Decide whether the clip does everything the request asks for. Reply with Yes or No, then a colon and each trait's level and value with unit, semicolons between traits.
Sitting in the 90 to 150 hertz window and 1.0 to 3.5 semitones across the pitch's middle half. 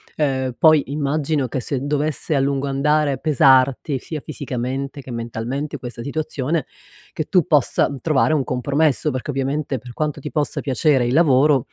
Yes: medium, 140 Hz; narrow, 2.6 semitones